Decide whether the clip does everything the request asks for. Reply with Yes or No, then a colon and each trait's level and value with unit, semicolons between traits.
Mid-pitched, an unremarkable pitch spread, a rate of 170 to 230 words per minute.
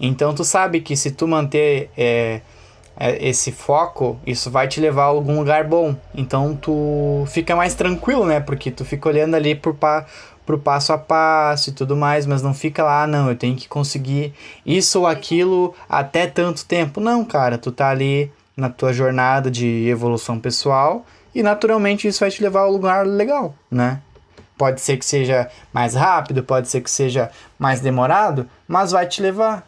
Yes: medium, 145 Hz; average, 4.1 semitones; fast, 185 wpm